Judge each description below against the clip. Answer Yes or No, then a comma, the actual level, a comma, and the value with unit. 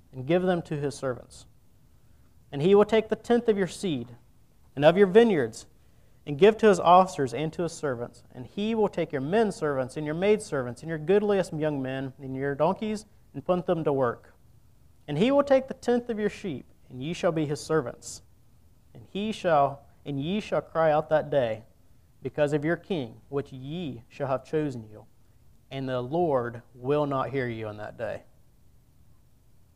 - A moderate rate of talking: Yes, average, 195 wpm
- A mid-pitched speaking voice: Yes, medium, 145 Hz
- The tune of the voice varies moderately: No, wide, 7.1 semitones